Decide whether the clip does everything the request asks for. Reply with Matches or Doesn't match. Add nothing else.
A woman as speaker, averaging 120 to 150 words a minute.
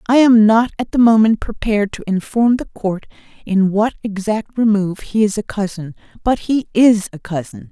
Doesn't match